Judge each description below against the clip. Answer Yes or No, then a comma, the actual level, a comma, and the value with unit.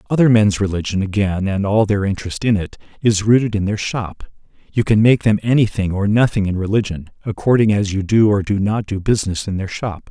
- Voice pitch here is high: No, low, 105 Hz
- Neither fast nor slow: No, fast, 215 wpm